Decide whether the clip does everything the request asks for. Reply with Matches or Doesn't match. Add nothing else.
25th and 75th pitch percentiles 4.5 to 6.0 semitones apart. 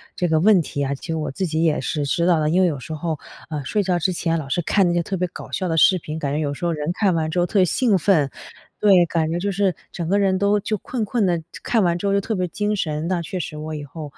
Doesn't match